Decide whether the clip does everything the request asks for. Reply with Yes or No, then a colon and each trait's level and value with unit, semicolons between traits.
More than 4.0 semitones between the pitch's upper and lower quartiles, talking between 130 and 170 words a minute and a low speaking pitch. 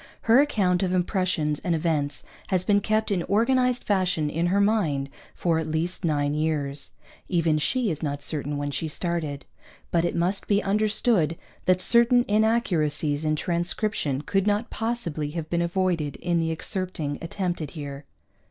No: average, 4.8 semitones; average, 160 wpm; medium, 170 Hz